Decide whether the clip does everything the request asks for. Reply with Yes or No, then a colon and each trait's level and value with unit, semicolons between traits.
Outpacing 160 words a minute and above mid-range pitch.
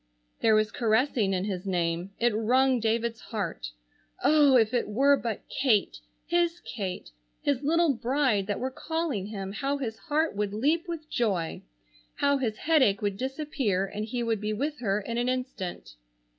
Yes: average, 170 wpm; high, 235 Hz